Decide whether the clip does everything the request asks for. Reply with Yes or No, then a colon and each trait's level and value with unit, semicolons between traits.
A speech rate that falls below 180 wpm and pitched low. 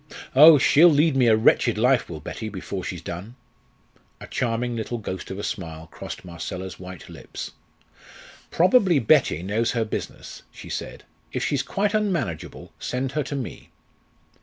Yes: average, 160 wpm; low, 115 Hz